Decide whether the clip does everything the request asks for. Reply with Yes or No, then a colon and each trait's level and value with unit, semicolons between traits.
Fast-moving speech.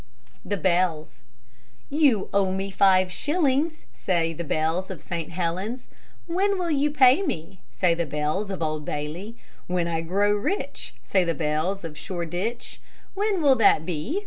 No: average, 155 wpm